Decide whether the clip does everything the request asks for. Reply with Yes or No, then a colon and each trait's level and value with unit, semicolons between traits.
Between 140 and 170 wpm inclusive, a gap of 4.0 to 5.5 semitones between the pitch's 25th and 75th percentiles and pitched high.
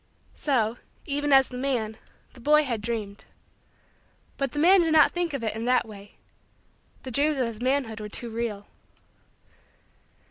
Yes: average, 165 wpm; average, 4.4 semitones; very high, 250 Hz